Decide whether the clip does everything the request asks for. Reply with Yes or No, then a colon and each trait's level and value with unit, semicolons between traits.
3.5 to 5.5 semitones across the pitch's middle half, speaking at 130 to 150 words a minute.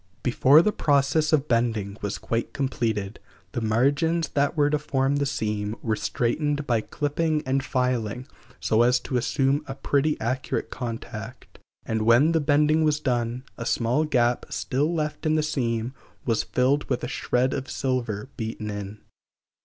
No: average, 4.0 semitones; average, 160 wpm